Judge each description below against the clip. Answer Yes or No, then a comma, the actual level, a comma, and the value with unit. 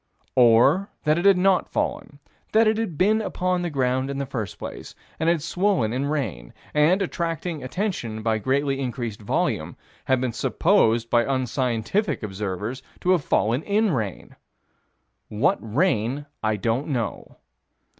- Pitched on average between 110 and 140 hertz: Yes, low, 135 Hz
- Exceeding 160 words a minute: No, average, 150 wpm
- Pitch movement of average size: No, wide, 7.5 semitones